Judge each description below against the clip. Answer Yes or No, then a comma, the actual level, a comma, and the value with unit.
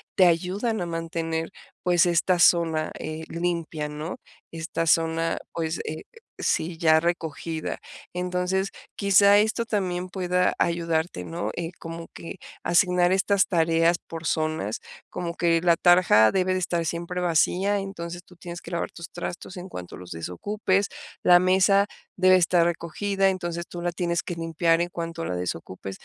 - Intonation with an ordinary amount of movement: No, narrow, 1.8 semitones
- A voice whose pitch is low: No, medium, 170 Hz